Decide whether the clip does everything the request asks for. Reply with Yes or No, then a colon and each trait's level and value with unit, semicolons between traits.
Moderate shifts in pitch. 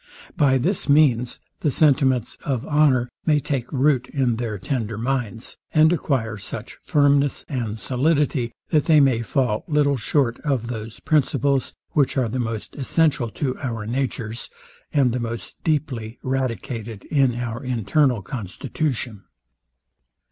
Yes: average, 3.6 semitones